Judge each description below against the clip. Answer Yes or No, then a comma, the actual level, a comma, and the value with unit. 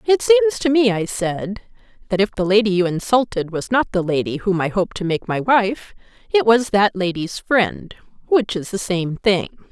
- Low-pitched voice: No, high, 205 Hz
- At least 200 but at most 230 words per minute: Yes, fast, 205 wpm